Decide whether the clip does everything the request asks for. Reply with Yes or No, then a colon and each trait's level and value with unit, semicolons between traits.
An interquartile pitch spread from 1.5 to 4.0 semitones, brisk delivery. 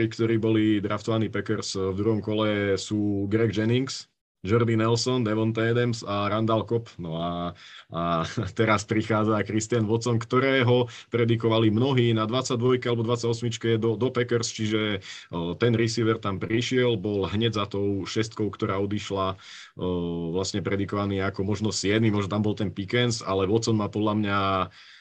No: narrow, 2.5 semitones; average, 150 wpm